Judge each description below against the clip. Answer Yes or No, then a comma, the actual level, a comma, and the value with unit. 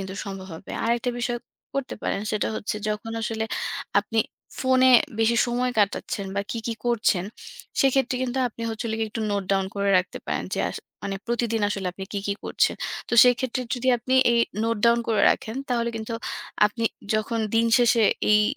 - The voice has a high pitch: Yes, high, 225 Hz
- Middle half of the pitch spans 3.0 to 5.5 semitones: No, narrow, 2.6 semitones